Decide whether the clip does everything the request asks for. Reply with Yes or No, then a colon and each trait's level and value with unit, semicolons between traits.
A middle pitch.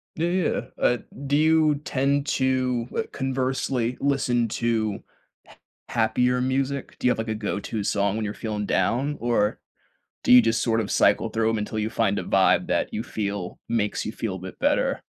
No: low, 115 Hz